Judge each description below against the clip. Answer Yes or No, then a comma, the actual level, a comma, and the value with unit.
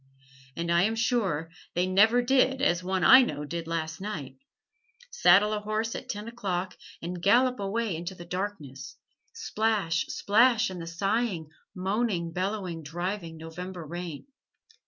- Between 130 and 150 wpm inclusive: Yes, average, 145 wpm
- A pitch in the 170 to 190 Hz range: Yes, medium, 185 Hz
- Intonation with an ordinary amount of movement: Yes, average, 4.3 semitones